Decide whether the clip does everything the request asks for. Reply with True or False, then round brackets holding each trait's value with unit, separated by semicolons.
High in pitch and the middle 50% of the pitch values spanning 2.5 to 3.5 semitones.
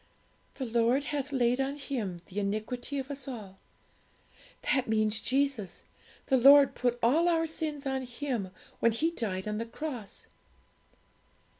False (255 Hz; 4.3 semitones)